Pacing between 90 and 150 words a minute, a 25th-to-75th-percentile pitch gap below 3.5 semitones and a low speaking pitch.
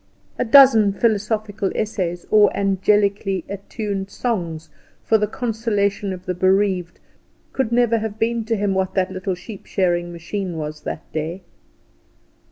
No: average, 140 wpm; average, 2.9 semitones; high, 200 Hz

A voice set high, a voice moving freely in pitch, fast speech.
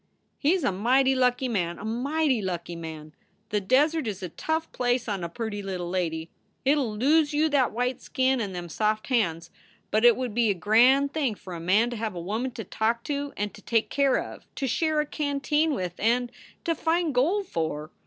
Yes: high, 235 Hz; wide, 6.4 semitones; fast, 215 wpm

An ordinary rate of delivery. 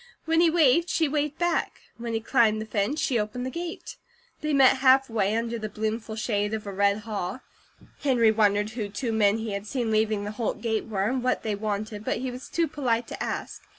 No: fast, 220 wpm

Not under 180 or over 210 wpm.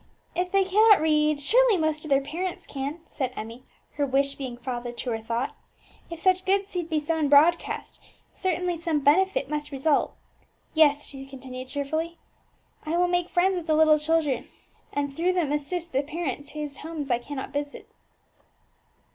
No: average, 170 wpm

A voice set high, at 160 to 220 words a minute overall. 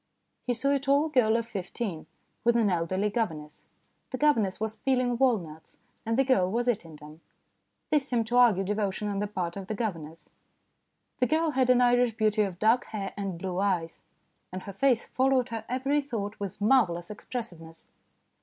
Yes: high, 220 Hz; average, 180 wpm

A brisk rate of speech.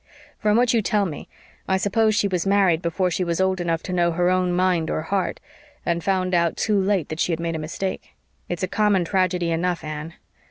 Yes: fast, 225 wpm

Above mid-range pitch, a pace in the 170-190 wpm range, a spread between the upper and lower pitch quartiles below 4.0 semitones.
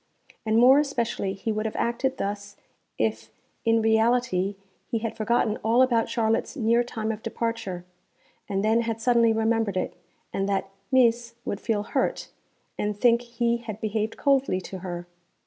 No: high, 225 Hz; average, 160 wpm; narrow, 2.5 semitones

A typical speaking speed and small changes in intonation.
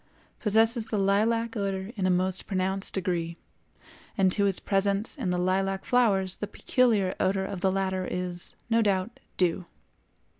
Yes: average, 155 wpm; narrow, 2.2 semitones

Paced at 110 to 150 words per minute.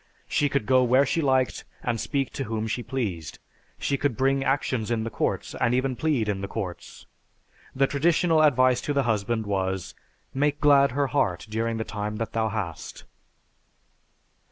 No: average, 175 wpm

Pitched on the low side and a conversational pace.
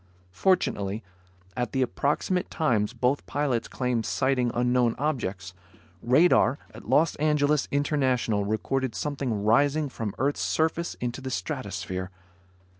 No: low, 130 Hz; slow, 115 wpm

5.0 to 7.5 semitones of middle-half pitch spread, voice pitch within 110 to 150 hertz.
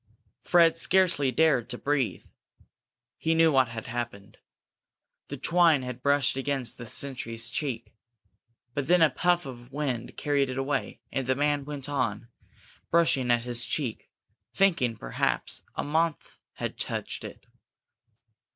No: average, 3.9 semitones; low, 135 Hz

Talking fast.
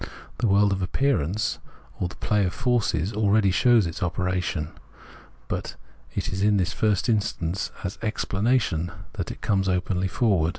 No: average, 155 wpm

